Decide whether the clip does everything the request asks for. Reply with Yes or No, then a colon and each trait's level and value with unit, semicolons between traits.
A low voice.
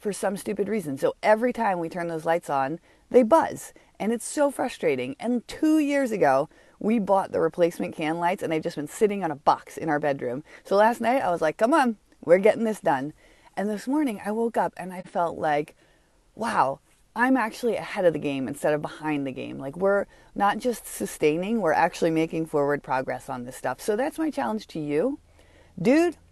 No: high, 195 Hz